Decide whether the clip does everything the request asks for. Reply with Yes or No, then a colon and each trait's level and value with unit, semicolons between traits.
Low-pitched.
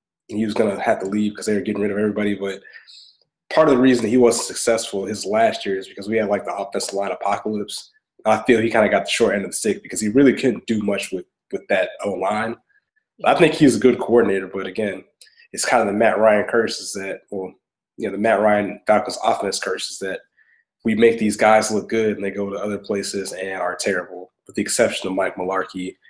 Yes: low, 105 Hz